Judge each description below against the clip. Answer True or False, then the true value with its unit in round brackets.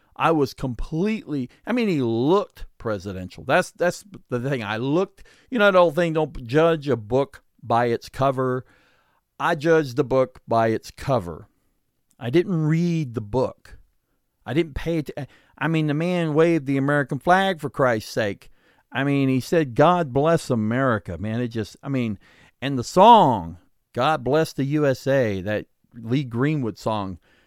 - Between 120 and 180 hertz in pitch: True (135 Hz)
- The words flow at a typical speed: True (170 wpm)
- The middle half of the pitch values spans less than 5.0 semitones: False (5.4 semitones)